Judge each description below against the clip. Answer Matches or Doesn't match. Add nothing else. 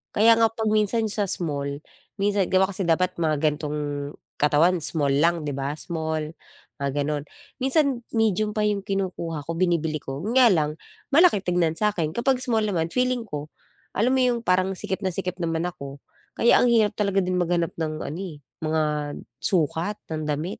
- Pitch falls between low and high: Matches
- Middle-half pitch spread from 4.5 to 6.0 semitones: Matches